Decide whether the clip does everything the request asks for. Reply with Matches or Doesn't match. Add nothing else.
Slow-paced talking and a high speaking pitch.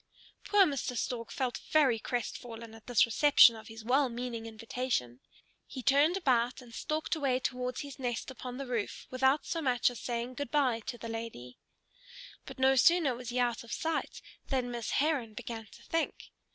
Doesn't match